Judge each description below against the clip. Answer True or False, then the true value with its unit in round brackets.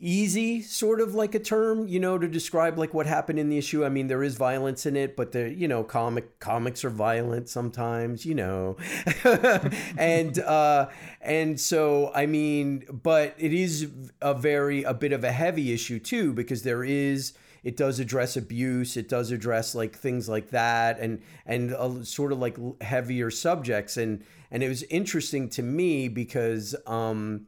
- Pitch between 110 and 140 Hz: True (135 Hz)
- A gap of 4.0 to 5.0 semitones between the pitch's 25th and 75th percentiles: True (4.5 semitones)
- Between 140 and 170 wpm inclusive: False (180 wpm)